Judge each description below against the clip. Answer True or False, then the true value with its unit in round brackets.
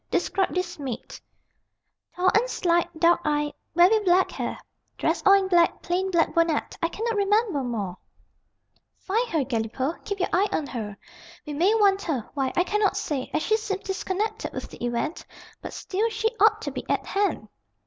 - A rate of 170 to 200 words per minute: True (180 wpm)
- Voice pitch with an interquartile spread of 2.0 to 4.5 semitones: False (5.4 semitones)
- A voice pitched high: True (355 Hz)